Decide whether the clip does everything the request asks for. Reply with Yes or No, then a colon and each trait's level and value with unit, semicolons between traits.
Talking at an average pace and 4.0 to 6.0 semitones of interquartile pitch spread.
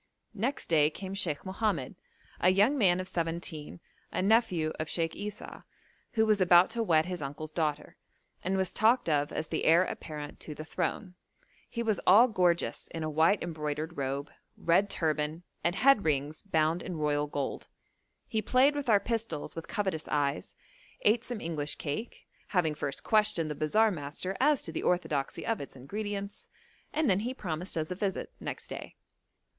Yes: average, 175 wpm; average, 5.1 semitones